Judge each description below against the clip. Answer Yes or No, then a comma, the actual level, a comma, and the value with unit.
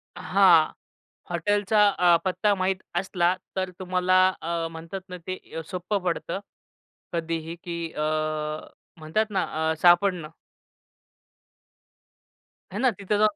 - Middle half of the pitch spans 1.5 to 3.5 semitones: Yes, narrow, 2.6 semitones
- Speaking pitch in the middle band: Yes, medium, 180 Hz